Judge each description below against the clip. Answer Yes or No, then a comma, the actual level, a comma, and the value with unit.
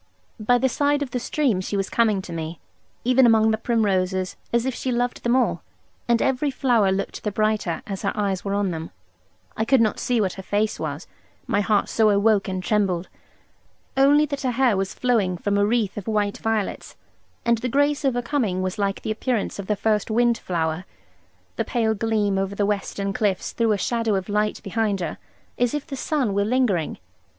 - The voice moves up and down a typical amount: Yes, average, 3.6 semitones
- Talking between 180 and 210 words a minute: Yes, fast, 205 wpm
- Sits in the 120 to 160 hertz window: No, high, 215 Hz